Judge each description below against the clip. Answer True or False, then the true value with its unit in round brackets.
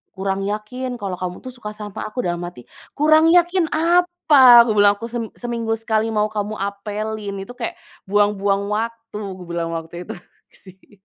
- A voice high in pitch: True (215 Hz)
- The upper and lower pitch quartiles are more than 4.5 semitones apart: False (3.6 semitones)